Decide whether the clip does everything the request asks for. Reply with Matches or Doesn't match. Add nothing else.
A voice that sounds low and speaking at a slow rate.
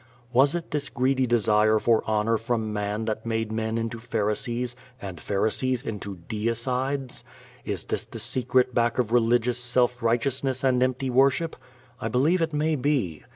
Doesn't match